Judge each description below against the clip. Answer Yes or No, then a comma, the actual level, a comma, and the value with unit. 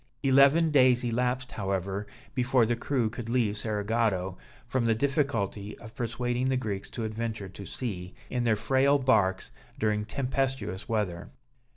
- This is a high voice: No, low, 115 Hz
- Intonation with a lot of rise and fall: No, average, 3.8 semitones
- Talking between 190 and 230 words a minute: No, average, 145 wpm